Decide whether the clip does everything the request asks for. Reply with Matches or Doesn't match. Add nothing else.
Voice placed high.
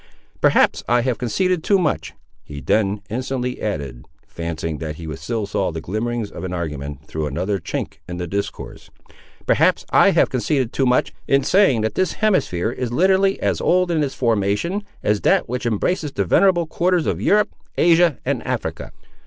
Doesn't match